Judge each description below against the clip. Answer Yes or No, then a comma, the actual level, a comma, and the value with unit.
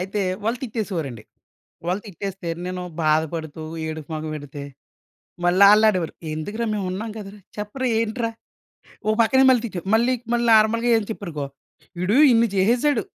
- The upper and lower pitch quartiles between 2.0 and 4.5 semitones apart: No, average, 5.3 semitones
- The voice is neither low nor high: No, high, 200 Hz